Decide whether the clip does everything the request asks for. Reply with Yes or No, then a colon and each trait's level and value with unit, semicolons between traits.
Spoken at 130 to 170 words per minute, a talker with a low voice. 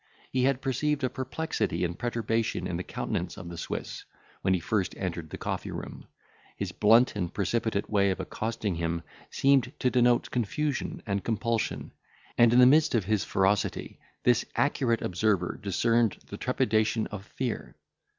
Yes: average, 160 wpm; low, 115 Hz